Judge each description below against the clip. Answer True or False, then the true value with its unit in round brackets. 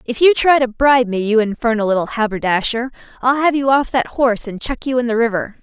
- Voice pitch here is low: False (240 Hz)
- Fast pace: True (235 wpm)